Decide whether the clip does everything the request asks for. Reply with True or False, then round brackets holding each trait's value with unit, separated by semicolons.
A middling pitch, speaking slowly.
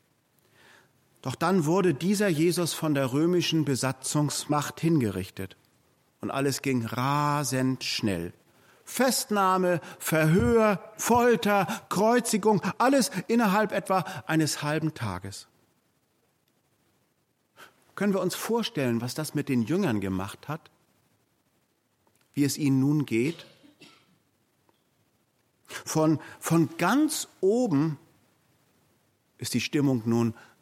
True (155 Hz; 95 wpm)